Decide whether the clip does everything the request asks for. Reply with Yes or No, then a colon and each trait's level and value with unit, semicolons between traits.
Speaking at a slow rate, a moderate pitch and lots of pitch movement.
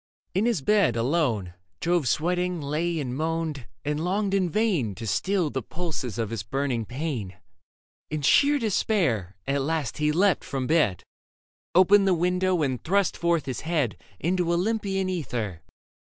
No: average, 150 wpm; medium, 160 Hz; wide, 6.0 semitones